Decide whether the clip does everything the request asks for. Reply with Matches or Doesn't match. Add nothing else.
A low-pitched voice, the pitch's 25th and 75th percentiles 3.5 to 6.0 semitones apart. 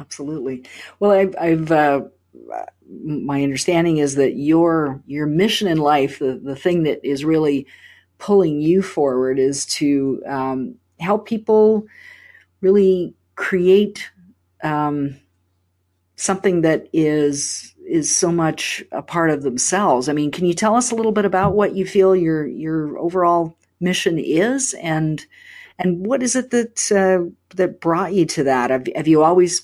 Doesn't match